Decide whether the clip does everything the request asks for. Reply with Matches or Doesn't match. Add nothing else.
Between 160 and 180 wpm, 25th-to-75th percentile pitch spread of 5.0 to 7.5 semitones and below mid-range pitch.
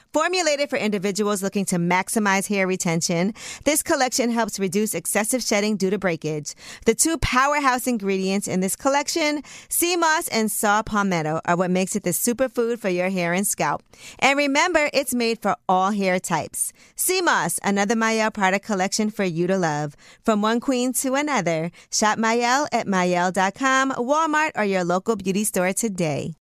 Doesn't match